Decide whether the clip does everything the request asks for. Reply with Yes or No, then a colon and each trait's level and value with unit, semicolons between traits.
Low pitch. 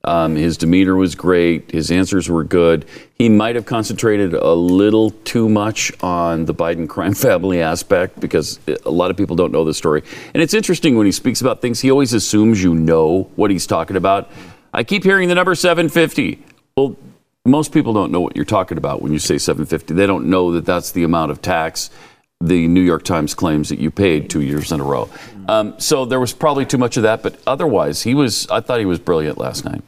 Yes: very low, 95 Hz